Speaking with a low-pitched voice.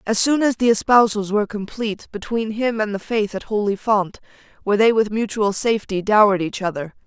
No: high, 210 Hz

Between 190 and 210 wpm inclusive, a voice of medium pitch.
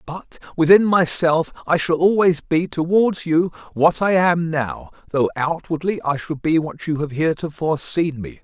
No: average, 170 wpm; medium, 160 Hz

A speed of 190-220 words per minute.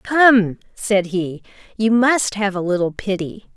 No: average, 150 wpm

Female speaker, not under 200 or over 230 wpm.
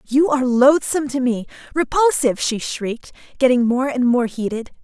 No: female; average, 160 wpm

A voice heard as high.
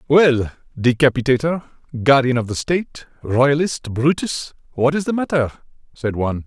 No: low, 135 Hz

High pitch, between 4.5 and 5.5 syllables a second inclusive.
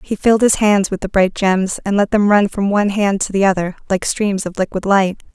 Yes: high, 200 Hz; 5.4 syllables/s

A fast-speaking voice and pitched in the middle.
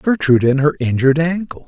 No: average, 180 wpm; medium, 150 Hz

